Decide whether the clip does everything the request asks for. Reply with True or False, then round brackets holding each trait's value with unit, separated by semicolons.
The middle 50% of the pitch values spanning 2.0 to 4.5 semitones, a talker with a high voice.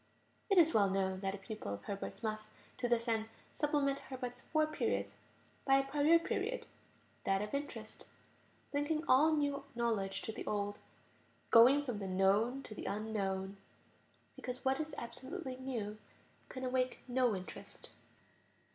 False (5.3 semitones; 245 Hz)